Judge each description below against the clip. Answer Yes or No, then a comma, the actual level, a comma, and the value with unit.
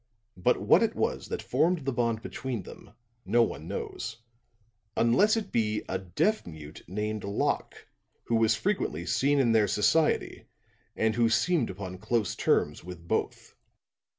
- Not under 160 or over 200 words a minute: No, average, 150 wpm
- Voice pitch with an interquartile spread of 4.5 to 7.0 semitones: Yes, wide, 5.4 semitones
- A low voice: Yes, low, 110 Hz